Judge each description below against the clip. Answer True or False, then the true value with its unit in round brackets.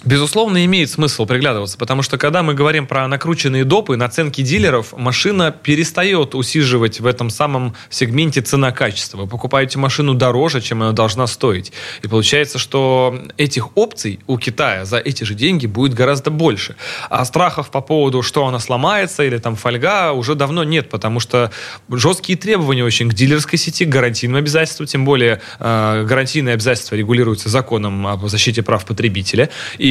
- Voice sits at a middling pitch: False (130 Hz)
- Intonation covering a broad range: False (4.1 semitones)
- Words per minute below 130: False (160 wpm)